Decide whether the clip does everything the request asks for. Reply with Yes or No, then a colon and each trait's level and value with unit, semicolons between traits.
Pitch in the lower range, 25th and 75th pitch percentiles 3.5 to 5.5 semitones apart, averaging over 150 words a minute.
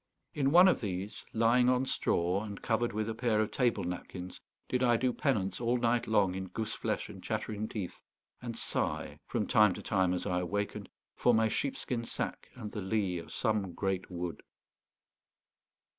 Yes: low, 110 Hz; average, 4.0 semitones; average, 180 wpm